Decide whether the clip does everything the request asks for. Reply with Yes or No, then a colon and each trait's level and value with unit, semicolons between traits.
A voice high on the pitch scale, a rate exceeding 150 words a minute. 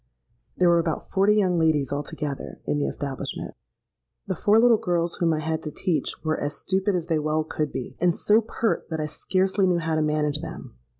No: medium, 165 Hz; fast, 205 wpm